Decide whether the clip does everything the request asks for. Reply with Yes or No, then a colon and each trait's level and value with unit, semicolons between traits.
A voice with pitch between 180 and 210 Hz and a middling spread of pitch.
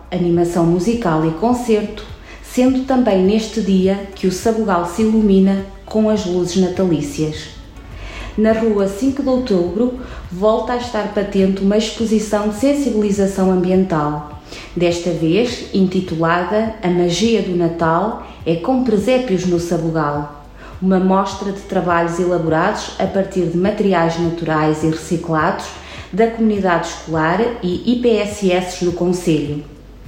Yes: high, 190 Hz; average, 4.1 semitones